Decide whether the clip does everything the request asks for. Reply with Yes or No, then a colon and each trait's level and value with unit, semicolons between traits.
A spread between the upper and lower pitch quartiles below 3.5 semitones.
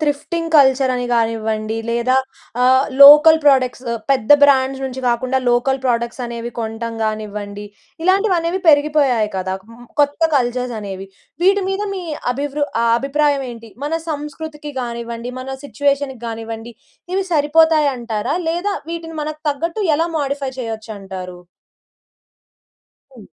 No: average, 4.4 semitones